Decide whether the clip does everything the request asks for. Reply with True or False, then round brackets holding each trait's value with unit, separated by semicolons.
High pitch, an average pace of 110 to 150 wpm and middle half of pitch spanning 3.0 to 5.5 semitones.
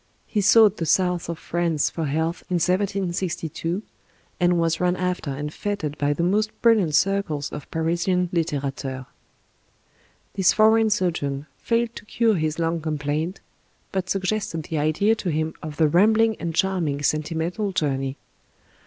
False (170 Hz; 145 wpm; 4.0 semitones)